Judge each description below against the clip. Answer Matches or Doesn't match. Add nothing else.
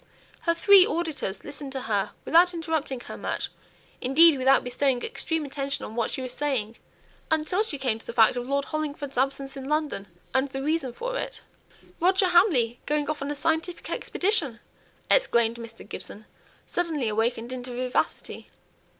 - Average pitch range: Matches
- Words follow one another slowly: Doesn't match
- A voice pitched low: Doesn't match